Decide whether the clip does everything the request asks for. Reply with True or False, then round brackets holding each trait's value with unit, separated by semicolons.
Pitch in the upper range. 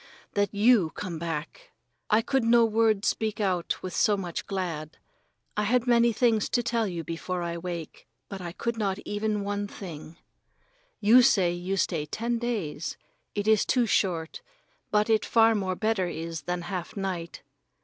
True (200 Hz)